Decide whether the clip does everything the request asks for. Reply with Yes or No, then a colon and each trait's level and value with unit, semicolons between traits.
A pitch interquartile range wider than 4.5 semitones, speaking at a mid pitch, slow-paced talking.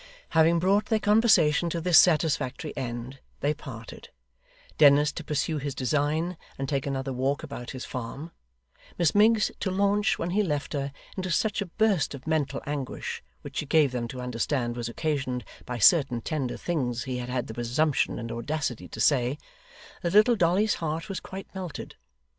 No: average, 5.2 semitones; medium, 150 Hz; average, 175 wpm